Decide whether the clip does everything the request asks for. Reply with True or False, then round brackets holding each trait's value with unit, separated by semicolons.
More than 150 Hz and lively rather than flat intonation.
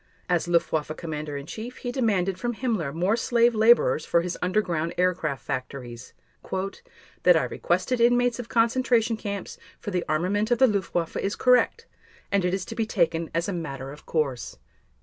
True (185 Hz; 6.0 semitones)